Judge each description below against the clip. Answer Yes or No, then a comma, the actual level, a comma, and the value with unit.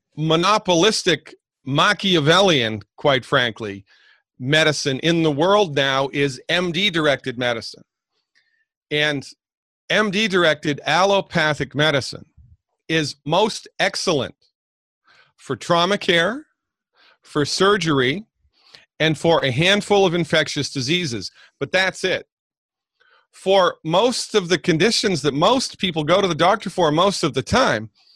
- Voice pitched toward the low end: No, medium, 165 Hz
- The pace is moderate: No, slow, 115 wpm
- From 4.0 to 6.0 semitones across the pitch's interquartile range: Yes, wide, 5.5 semitones